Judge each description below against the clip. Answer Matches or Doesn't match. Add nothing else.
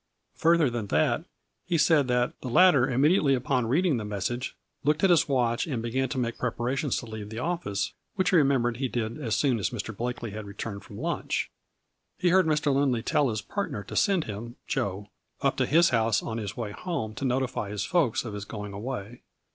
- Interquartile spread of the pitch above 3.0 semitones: Matches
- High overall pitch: Doesn't match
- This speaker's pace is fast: Matches